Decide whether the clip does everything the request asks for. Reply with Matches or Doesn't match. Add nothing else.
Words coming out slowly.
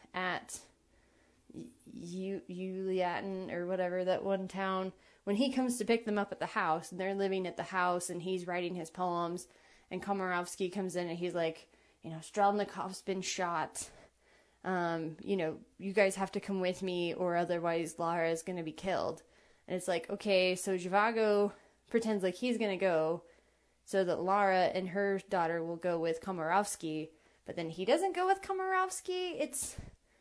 Doesn't match